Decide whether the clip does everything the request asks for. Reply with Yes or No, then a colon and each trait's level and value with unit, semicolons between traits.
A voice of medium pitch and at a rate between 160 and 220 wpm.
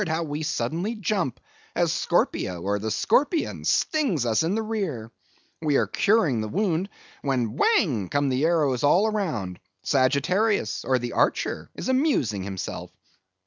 No: medium, 150 Hz; average, 145 wpm